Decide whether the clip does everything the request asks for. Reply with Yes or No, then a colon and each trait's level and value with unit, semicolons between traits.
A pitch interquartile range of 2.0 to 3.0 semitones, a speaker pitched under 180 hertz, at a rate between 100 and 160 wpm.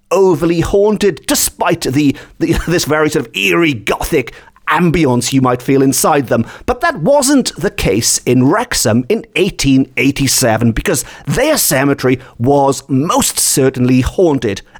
No: average, 5.1 semitones; medium, 140 Hz; slow, 135 wpm